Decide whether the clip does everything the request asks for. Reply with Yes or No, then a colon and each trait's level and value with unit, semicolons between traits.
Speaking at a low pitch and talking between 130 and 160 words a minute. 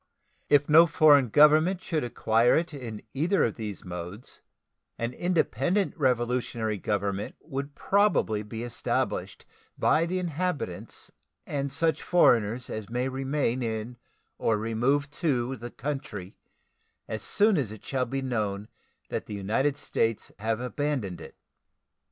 Yes: low, 125 Hz; slow, 135 wpm